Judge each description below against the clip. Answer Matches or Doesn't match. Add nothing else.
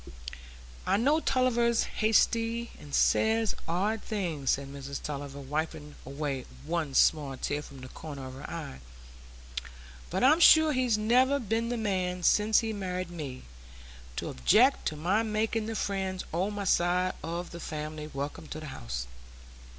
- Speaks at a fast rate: Doesn't match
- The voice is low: Doesn't match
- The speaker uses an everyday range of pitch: Doesn't match